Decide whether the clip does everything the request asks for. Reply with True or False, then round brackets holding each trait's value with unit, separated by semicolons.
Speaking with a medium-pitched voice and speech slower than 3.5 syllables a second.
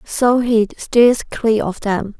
False (225 Hz; 3.0 syllables/s)